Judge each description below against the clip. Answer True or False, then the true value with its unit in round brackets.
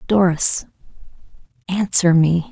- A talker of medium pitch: True (170 Hz)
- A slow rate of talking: True (70 wpm)